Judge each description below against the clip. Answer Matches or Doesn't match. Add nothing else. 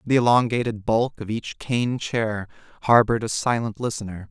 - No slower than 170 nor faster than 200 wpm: Doesn't match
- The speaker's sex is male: Matches